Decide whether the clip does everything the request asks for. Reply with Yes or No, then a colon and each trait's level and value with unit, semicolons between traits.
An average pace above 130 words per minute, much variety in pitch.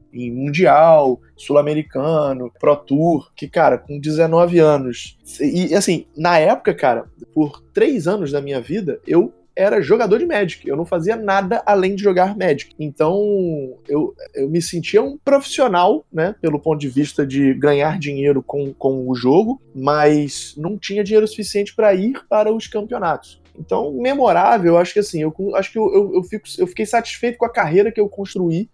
Yes: average, 175 wpm; wide, 6.5 semitones